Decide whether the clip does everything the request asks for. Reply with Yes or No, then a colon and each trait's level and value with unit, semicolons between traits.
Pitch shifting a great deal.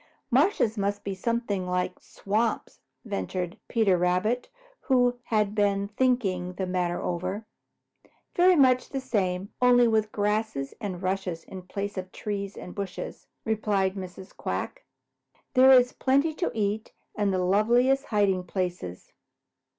No: average, 4.2 semitones